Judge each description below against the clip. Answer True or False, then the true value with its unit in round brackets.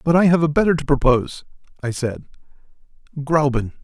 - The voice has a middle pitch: True (150 Hz)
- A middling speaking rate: True (155 wpm)